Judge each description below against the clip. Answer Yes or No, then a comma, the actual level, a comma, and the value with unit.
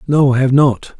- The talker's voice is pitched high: No, low, 135 Hz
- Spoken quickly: Yes, fast, 240 wpm